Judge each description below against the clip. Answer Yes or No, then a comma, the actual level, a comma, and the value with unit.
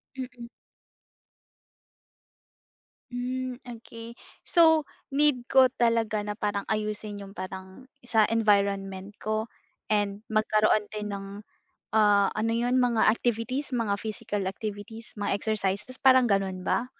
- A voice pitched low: No, high, 215 Hz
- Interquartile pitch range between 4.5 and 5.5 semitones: No, average, 3.1 semitones